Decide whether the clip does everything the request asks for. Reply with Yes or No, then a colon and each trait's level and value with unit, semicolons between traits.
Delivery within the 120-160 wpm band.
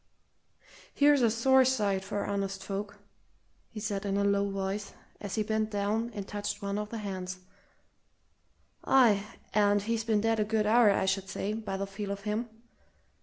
No: average, 175 wpm